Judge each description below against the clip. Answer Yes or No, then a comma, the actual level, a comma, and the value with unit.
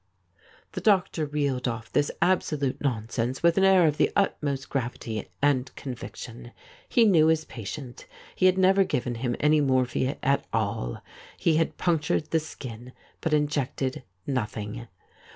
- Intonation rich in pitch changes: No, average, 4.5 semitones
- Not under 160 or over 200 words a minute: No, average, 150 wpm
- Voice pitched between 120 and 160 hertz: Yes, medium, 140 Hz